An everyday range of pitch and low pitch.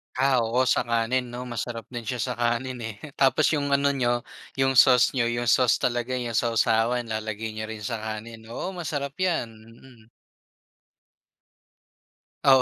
No: narrow, 2.3 semitones; low, 120 Hz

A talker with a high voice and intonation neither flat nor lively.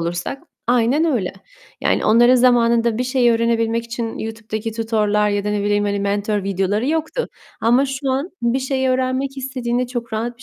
Yes: high, 235 Hz; average, 3.1 semitones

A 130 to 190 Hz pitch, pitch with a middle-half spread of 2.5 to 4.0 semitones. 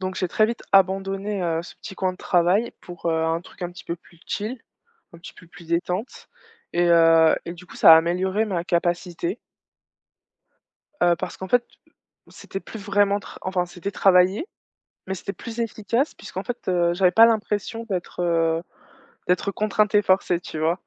Yes: medium, 185 Hz; average, 2.9 semitones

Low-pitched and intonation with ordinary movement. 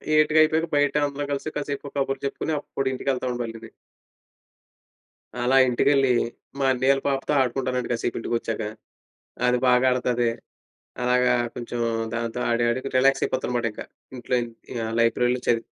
No: low, 125 Hz; narrow, 2.3 semitones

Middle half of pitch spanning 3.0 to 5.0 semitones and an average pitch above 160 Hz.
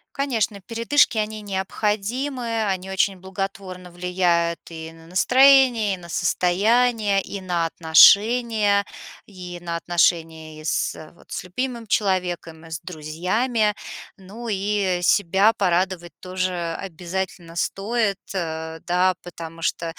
Yes: average, 3.6 semitones; high, 190 Hz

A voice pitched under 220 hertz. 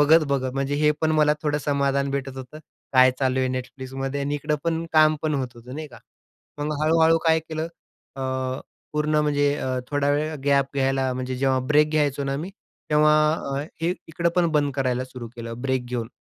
Yes: medium, 140 Hz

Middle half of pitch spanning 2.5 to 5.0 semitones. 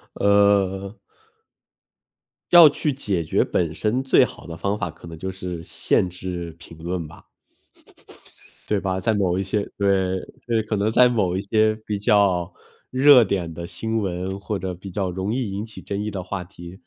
Yes: average, 2.9 semitones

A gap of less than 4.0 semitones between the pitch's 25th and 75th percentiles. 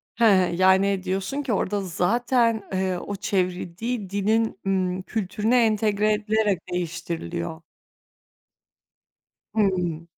Yes: average, 3.1 semitones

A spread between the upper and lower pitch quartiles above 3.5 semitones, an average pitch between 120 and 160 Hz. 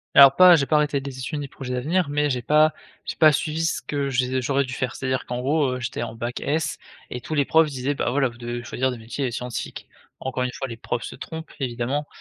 No: average, 2.9 semitones; low, 135 Hz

